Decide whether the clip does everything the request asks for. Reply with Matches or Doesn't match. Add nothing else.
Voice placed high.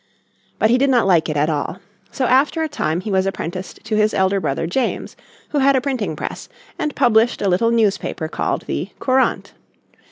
Matches